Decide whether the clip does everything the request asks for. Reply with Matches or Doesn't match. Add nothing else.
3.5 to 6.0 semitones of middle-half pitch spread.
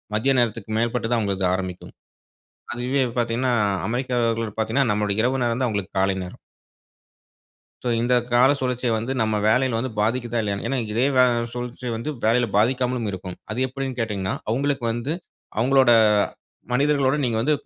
Doesn't match